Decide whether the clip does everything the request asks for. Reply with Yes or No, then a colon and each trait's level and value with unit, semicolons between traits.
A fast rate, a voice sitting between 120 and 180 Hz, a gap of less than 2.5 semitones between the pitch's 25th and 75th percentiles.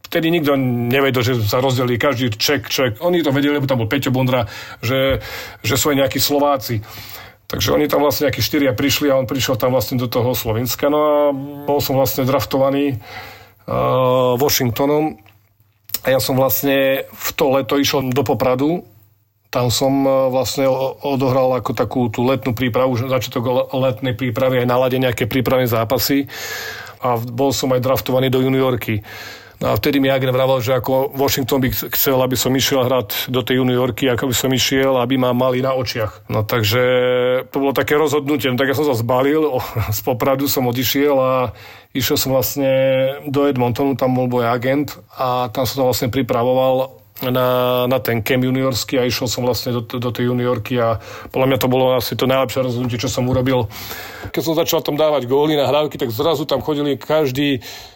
Yes: fast, 185 wpm; low, 130 Hz; narrow, 1.7 semitones